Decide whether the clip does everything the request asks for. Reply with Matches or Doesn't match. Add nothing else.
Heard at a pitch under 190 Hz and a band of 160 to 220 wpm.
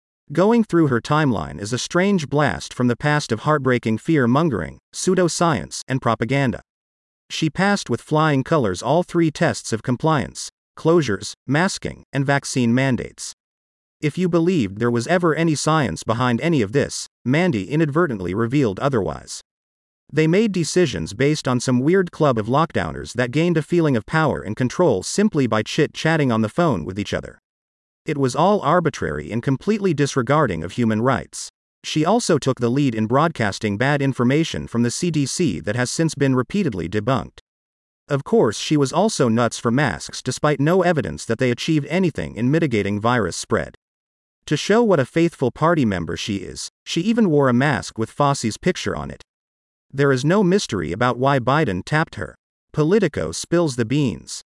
Matches